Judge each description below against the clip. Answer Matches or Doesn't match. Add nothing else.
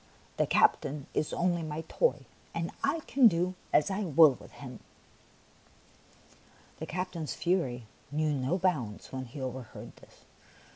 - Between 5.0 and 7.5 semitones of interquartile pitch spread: Matches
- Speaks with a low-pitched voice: Doesn't match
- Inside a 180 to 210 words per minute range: Doesn't match